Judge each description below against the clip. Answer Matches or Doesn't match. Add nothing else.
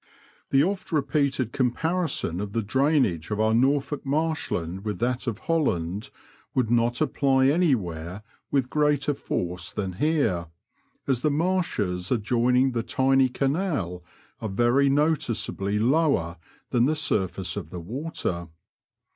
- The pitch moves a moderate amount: Doesn't match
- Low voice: Matches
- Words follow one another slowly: Matches